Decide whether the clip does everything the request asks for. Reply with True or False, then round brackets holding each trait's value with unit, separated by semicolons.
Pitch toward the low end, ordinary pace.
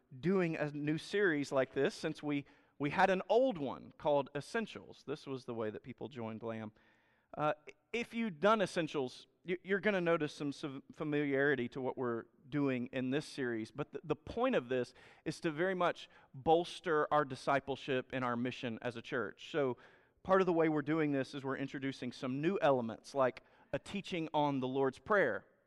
False (145 Hz; 190 wpm)